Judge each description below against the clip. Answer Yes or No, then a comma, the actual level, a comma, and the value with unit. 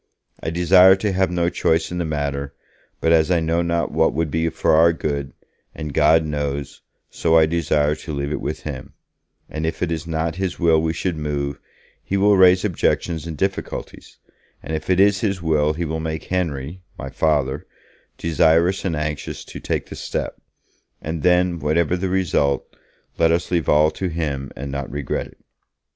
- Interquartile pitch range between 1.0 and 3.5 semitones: Yes, average, 2.7 semitones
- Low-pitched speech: Yes, very low, 80 Hz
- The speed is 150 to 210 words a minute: Yes, average, 185 wpm